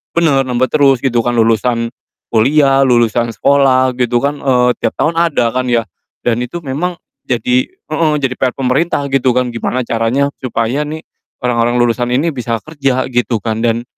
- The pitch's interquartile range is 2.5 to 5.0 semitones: Yes, average, 2.8 semitones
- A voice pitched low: Yes, low, 125 Hz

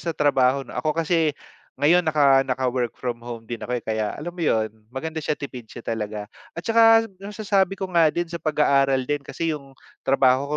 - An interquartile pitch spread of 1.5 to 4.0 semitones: No, average, 4.7 semitones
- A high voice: No, medium, 140 Hz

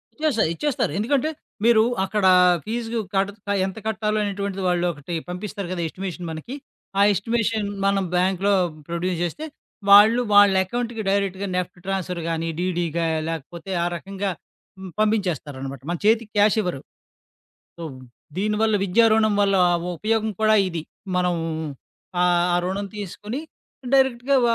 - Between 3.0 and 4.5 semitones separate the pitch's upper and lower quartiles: Yes, average, 3.5 semitones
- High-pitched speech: Yes, high, 200 Hz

